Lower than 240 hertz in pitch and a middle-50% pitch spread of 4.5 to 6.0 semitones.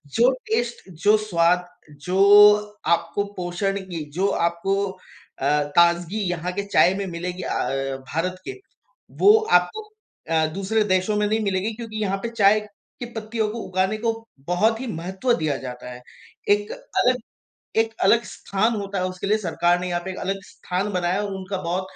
No: high, 190 Hz; average, 3.5 semitones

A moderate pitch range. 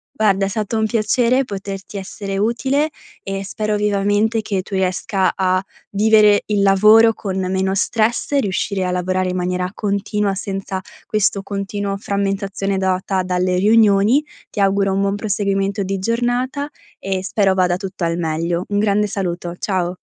No: narrow, 2.0 semitones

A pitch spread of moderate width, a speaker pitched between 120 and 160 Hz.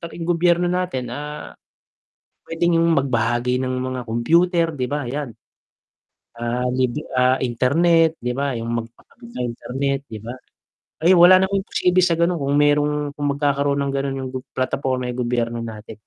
Yes: average, 5.0 semitones; medium, 140 Hz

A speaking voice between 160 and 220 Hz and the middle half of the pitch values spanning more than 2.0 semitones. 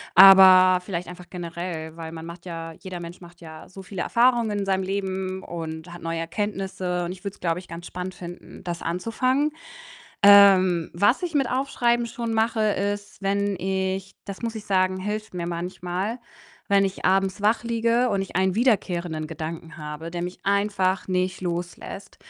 Yes: medium, 185 Hz; average, 2.7 semitones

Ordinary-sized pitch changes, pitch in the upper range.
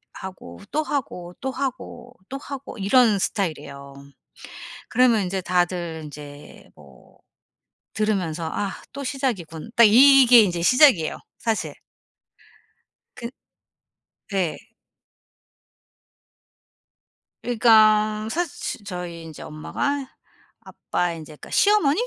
No: wide, 6.9 semitones; high, 210 Hz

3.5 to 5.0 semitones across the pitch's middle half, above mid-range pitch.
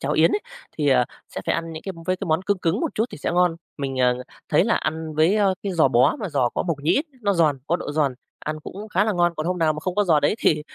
No: average, 3.8 semitones; medium, 165 Hz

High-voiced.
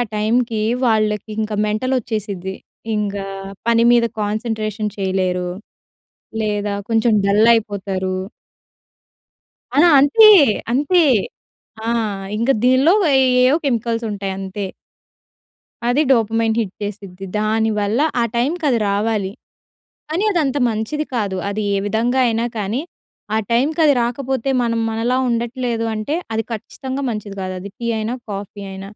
Yes: high, 220 Hz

